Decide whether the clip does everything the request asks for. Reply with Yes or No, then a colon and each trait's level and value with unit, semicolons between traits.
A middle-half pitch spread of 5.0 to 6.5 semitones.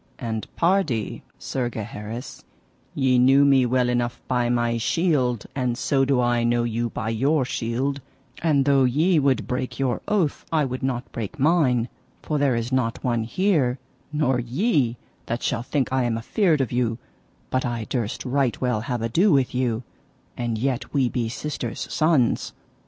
No: average, 2.9 semitones